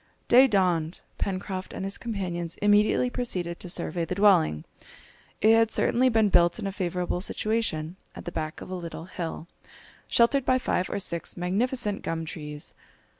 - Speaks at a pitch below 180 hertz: No, medium, 185 Hz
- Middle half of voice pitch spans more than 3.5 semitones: Yes, average, 4.2 semitones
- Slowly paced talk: No, average, 165 wpm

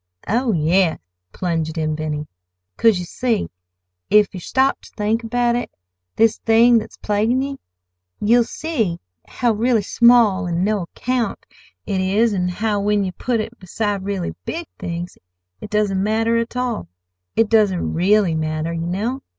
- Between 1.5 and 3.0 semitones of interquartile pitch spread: No, average, 5.1 semitones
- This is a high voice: Yes, high, 205 Hz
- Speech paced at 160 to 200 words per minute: No, average, 150 wpm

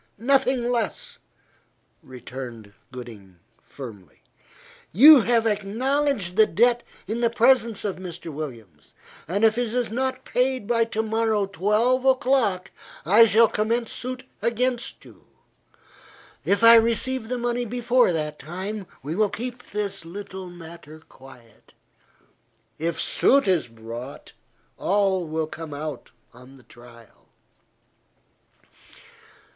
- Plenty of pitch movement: Yes, wide, 7.3 semitones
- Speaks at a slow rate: Yes, slow, 120 wpm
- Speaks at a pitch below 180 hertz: No, high, 205 Hz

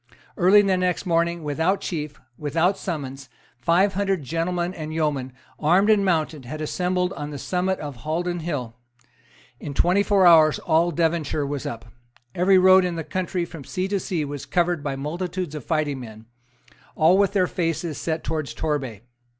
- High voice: No, medium, 165 Hz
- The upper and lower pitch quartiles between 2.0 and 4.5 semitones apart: Yes, average, 3.6 semitones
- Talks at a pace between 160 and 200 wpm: Yes, average, 170 wpm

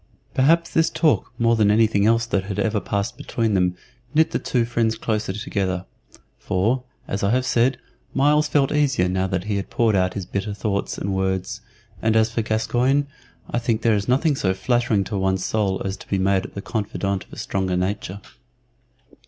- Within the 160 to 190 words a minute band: No, average, 200 wpm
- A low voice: Yes, low, 105 Hz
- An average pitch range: Yes, average, 3.6 semitones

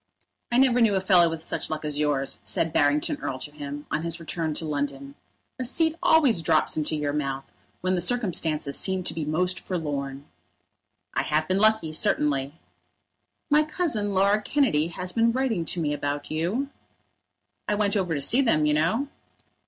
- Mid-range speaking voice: Yes, medium, 165 Hz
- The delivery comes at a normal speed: Yes, average, 180 wpm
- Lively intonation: Yes, wide, 5.9 semitones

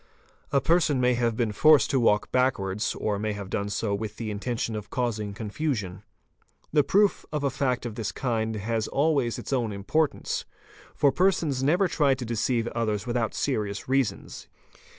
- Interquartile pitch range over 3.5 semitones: Yes, average, 4.5 semitones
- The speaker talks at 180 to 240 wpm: No, average, 170 wpm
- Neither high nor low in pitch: No, low, 120 Hz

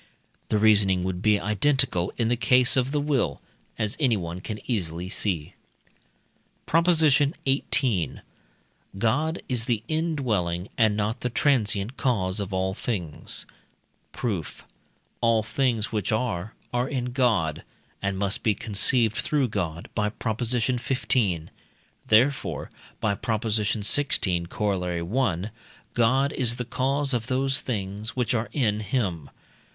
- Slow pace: Yes, slow, 130 wpm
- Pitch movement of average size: Yes, average, 4.6 semitones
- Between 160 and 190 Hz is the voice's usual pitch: No, low, 110 Hz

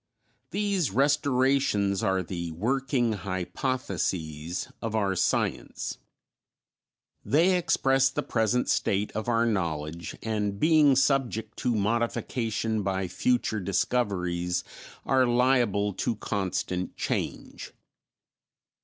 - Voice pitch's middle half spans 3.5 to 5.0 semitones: No, wide, 5.4 semitones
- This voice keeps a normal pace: No, slow, 95 wpm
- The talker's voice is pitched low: Yes, low, 110 Hz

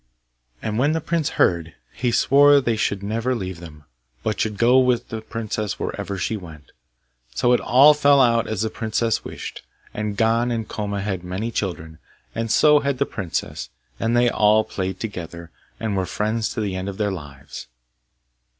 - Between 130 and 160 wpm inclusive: No, average, 180 wpm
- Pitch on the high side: No, low, 110 Hz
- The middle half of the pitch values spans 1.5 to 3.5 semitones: No, average, 4.0 semitones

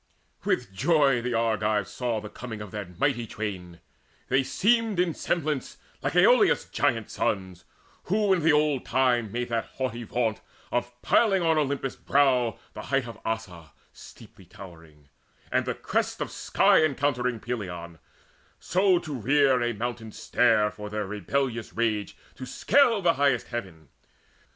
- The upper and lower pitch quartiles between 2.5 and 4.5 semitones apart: No, average, 5.0 semitones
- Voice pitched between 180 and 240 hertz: No, low, 120 Hz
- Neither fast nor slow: Yes, average, 150 wpm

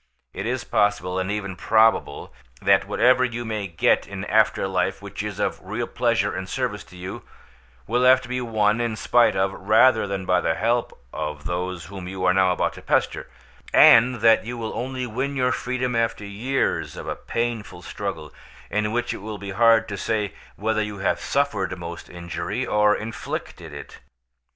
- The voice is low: Yes, low, 105 Hz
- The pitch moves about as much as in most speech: Yes, average, 3.8 semitones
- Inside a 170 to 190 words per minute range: Yes, average, 185 wpm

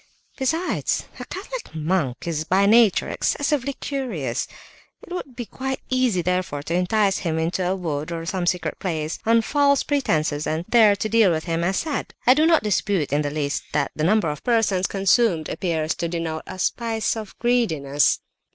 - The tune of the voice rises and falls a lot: Yes, wide, 6.8 semitones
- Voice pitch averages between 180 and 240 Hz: Yes, medium, 185 Hz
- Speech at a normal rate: Yes, average, 185 wpm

